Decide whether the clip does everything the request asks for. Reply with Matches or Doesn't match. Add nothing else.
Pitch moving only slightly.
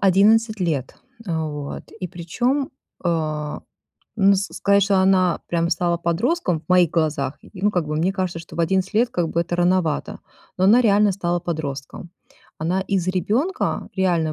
Doesn't match